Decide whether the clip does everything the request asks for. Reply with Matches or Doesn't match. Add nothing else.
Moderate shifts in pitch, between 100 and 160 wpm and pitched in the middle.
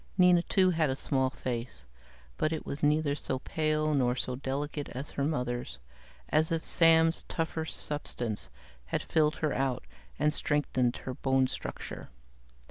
Matches